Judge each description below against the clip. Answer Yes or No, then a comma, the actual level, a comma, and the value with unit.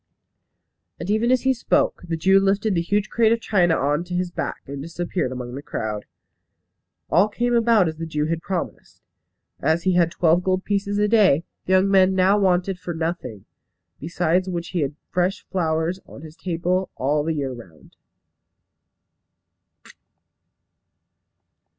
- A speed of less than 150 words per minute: No, average, 160 wpm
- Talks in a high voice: No, medium, 175 Hz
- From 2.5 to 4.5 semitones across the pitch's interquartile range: Yes, average, 3.5 semitones